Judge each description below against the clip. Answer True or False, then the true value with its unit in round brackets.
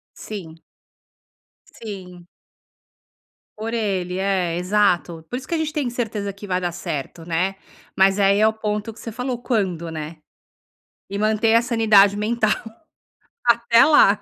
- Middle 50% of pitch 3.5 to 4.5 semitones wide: True (3.9 semitones)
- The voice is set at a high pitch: True (205 Hz)